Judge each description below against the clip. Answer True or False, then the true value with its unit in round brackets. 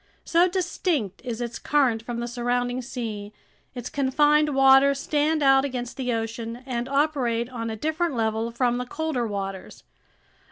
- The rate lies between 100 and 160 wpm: True (155 wpm)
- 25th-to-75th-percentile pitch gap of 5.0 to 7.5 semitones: False (3.4 semitones)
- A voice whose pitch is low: False (250 Hz)